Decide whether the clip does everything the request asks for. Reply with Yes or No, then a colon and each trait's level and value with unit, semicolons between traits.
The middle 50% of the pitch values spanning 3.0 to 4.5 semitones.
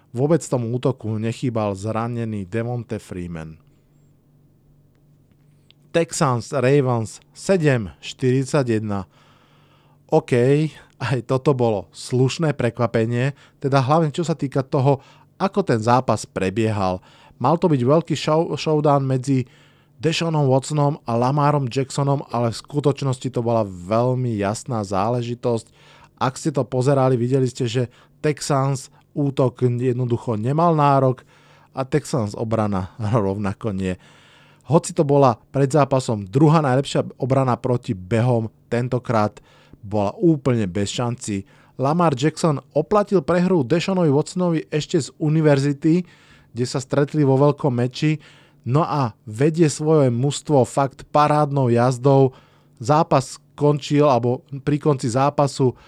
Yes: average, 3.6 semitones